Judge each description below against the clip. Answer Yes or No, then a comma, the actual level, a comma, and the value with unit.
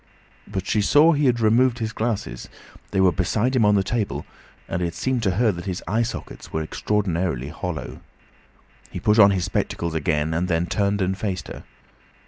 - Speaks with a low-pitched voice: Yes, low, 100 Hz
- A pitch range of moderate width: Yes, average, 4.4 semitones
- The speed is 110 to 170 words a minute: No, average, 190 wpm